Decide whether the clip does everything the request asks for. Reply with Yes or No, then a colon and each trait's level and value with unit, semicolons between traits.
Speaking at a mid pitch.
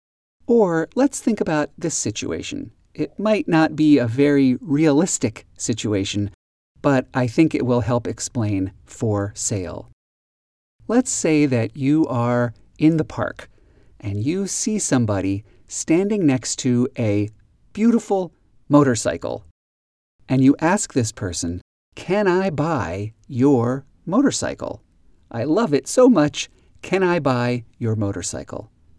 No: low, 125 Hz